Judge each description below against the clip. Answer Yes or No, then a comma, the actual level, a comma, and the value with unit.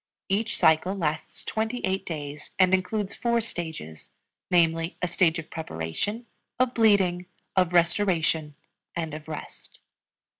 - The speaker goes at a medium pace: No, slow, 125 wpm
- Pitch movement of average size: Yes, average, 4.0 semitones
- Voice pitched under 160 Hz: No, medium, 175 Hz